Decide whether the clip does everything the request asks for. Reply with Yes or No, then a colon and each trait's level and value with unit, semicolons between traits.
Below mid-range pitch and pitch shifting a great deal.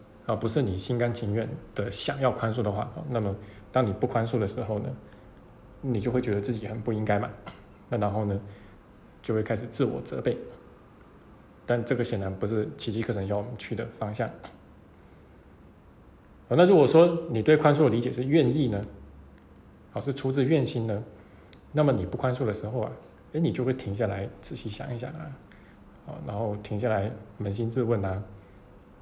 No: low, 110 Hz; average, 3.6 semitones